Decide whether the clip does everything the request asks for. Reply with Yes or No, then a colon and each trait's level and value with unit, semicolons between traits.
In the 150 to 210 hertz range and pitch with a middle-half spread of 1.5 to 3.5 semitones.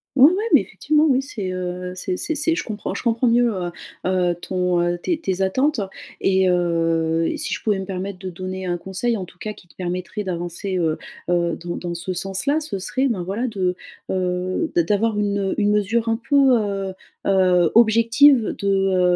No: high, 190 Hz; average, 3.9 semitones